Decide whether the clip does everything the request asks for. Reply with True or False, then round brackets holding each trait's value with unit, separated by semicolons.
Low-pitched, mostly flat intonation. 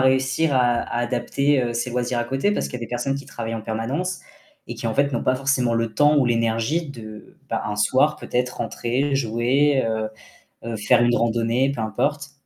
False (125 Hz; 3.1 semitones)